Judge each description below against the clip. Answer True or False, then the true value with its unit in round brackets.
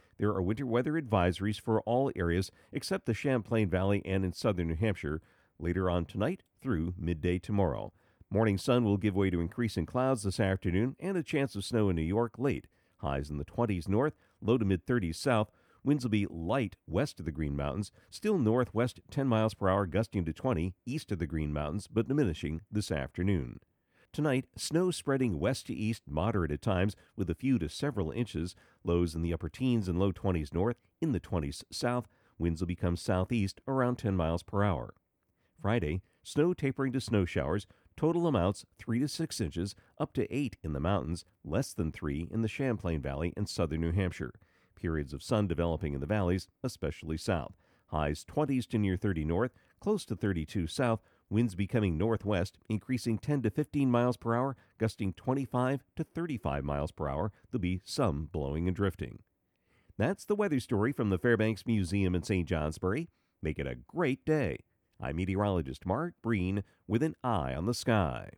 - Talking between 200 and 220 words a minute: False (185 wpm)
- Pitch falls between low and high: False (100 Hz)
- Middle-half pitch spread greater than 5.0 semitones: True (5.5 semitones)